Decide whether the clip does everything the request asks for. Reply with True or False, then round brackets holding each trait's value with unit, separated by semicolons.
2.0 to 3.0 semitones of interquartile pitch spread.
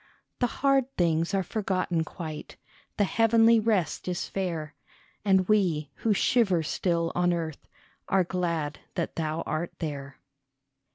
False (4.0 semitones)